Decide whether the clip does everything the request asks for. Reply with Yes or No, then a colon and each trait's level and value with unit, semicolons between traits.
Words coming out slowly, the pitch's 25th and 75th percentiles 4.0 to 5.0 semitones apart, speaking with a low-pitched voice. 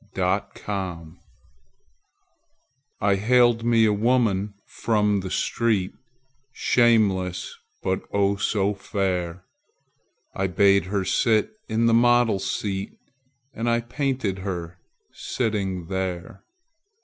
No: slow, 100 wpm; average, 3.4 semitones; low, 100 Hz